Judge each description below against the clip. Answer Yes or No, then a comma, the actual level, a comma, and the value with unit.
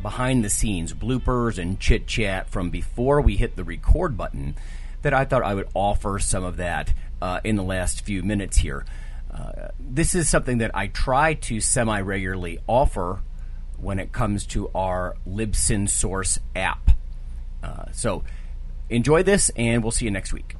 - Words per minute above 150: Yes, average, 170 wpm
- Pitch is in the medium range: No, very low, 95 Hz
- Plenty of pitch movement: Yes, wide, 7.7 semitones